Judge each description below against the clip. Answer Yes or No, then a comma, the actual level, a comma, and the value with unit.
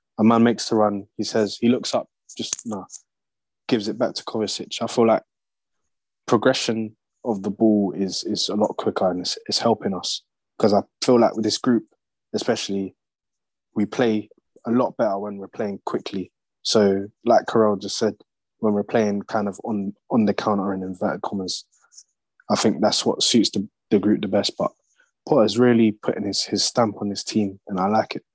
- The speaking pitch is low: Yes, low, 105 Hz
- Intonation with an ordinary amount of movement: No, narrow, 2.1 semitones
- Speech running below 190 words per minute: No, average, 200 wpm